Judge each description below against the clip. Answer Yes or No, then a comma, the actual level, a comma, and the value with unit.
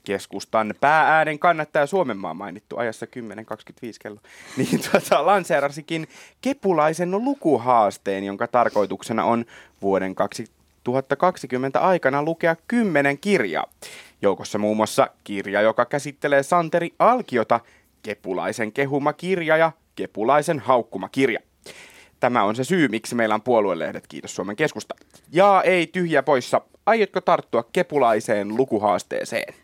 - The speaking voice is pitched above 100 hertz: Yes, medium, 140 Hz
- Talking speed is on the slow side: No, average, 110 wpm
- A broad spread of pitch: Yes, wide, 7.8 semitones